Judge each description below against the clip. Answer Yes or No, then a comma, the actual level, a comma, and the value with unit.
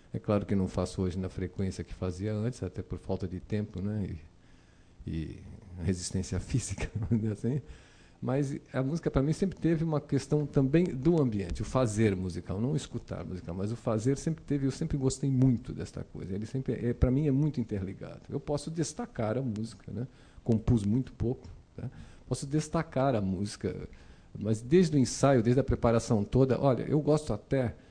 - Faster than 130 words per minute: Yes, fast, 185 wpm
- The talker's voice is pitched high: No, low, 115 Hz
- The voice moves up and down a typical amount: No, wide, 6.1 semitones